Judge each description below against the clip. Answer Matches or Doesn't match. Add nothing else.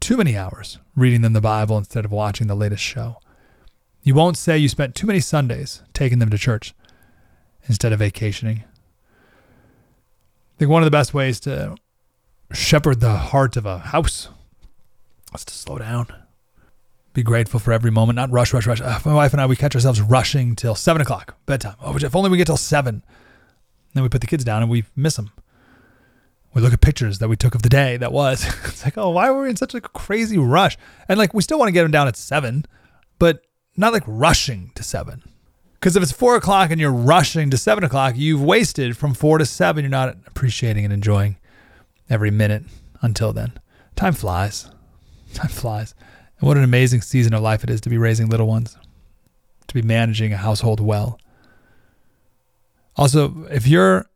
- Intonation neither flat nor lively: Matches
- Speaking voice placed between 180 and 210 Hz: Doesn't match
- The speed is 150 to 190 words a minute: Doesn't match